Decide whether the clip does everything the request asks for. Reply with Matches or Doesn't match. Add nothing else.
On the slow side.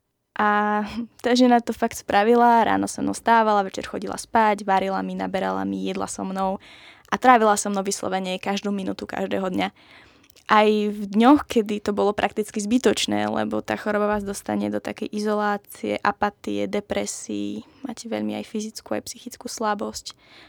Doesn't match